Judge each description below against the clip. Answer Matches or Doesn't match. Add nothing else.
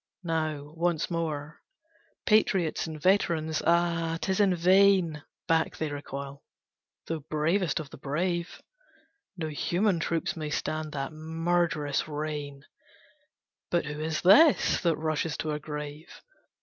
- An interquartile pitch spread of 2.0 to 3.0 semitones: Matches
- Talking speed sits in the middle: Doesn't match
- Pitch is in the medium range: Matches